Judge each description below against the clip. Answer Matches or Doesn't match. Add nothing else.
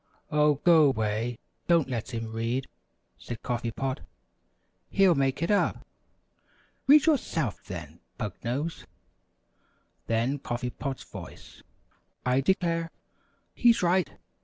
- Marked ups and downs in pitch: Matches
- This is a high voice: Doesn't match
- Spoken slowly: Matches